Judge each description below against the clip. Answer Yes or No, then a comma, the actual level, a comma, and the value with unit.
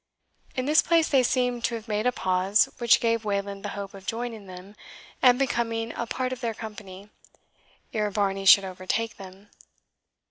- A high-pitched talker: Yes, high, 220 Hz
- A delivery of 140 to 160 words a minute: No, average, 175 wpm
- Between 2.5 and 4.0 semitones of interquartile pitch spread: Yes, average, 3.4 semitones